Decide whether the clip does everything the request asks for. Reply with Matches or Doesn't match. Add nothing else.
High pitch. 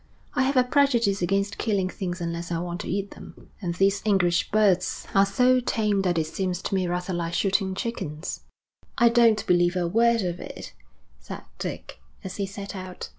Matches